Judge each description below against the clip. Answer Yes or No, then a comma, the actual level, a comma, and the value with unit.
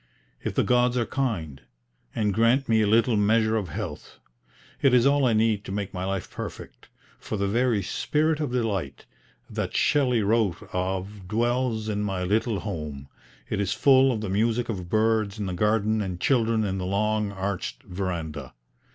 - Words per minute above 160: Yes, average, 175 wpm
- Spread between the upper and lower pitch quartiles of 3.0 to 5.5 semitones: Yes, average, 3.3 semitones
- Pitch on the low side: Yes, low, 105 Hz